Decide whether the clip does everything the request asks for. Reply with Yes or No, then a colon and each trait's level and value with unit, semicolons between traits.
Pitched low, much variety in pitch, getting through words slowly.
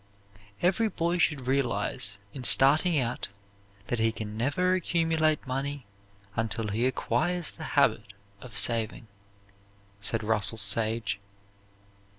Yes: low, 125 Hz; wide, 6.0 semitones; slow, 115 wpm